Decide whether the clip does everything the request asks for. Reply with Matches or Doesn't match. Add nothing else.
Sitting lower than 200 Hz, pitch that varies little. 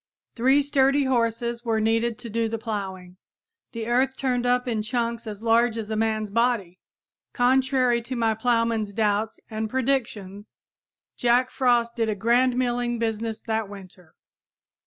Doesn't match